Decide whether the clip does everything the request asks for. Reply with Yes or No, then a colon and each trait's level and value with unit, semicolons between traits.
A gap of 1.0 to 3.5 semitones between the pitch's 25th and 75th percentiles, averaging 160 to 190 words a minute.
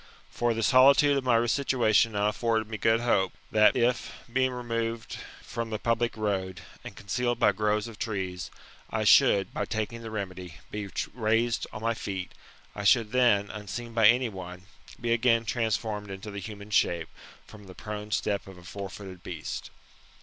Yes: narrow, 2.6 semitones; average, 170 wpm